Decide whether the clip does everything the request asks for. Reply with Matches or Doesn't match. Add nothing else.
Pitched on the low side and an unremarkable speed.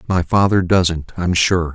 Matches